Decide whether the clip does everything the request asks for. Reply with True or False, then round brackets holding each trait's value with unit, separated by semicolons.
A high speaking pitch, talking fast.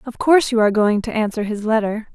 True (220 Hz; 250 wpm)